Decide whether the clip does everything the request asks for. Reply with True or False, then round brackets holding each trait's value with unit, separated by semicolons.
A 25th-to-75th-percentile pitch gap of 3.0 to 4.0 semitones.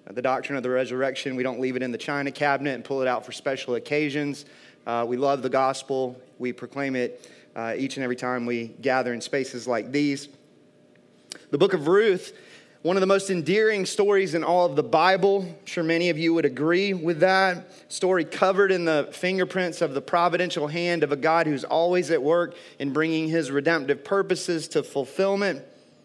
False (5.4 semitones)